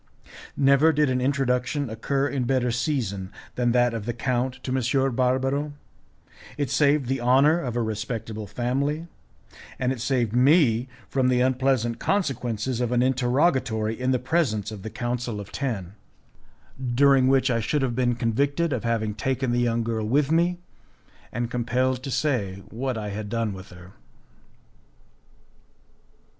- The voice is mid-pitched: No, low, 125 Hz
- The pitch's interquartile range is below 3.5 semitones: Yes, average, 2.8 semitones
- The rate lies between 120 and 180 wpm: Yes, average, 155 wpm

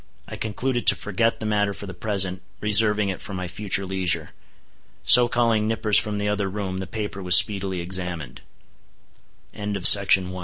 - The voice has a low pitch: Yes, low, 100 Hz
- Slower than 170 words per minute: No, average, 185 wpm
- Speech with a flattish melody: Yes, narrow, 2.3 semitones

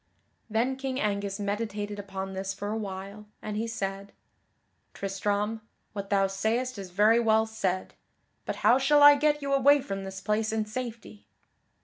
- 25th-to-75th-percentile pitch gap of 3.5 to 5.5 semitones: No, average, 2.7 semitones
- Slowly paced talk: No, average, 160 wpm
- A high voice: Yes, high, 210 Hz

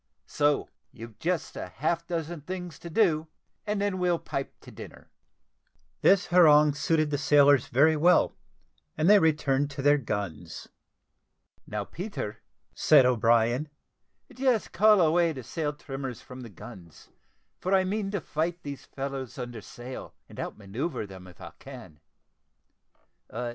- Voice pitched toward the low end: No, medium, 145 Hz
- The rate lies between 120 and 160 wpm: Yes, average, 145 wpm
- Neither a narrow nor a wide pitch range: No, wide, 5.9 semitones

